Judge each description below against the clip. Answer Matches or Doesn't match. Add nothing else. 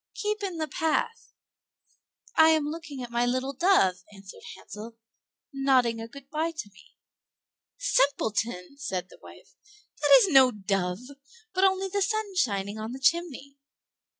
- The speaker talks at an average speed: Matches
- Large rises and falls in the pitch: Matches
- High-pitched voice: Matches